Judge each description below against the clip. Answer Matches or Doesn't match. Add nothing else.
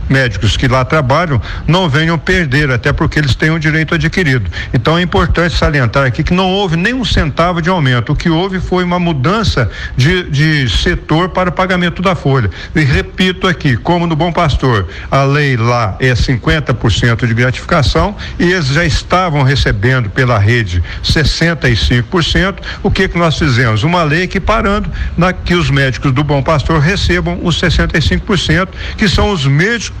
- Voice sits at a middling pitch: Matches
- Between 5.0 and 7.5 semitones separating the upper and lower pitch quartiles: Matches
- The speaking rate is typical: Matches